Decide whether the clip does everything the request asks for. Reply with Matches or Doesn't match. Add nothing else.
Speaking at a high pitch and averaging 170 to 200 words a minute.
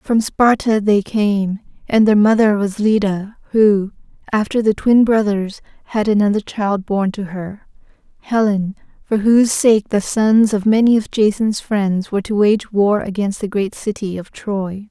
Doesn't match